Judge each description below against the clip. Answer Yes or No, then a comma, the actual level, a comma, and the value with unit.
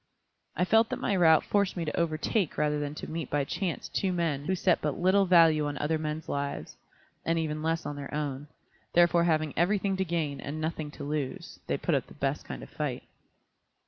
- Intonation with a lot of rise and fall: No, average, 2.8 semitones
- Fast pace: Yes, fast, 215 wpm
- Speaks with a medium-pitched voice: Yes, medium, 160 Hz